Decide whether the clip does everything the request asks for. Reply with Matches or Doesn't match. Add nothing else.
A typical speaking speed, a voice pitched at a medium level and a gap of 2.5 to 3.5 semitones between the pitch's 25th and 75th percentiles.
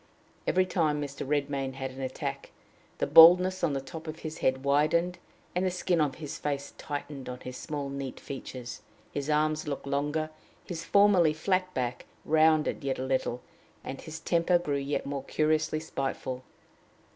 Matches